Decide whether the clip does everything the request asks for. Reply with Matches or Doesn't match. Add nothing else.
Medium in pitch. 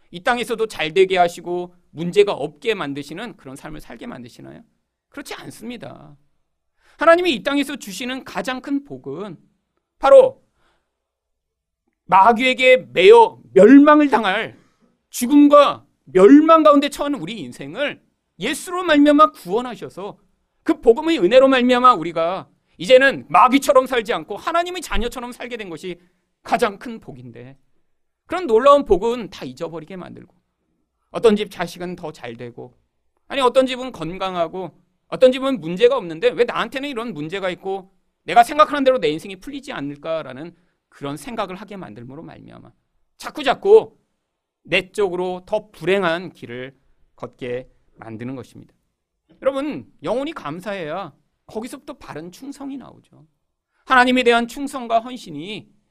Doesn't match